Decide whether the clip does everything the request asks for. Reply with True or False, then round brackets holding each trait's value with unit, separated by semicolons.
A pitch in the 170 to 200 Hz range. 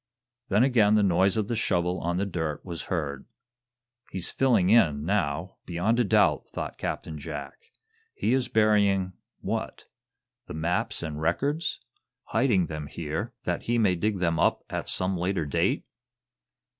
False (90 Hz)